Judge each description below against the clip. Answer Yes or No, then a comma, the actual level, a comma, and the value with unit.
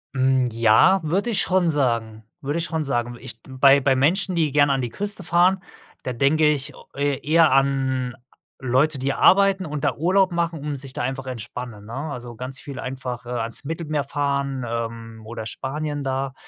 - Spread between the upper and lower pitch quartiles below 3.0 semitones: No, average, 3.8 semitones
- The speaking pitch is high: No, low, 135 Hz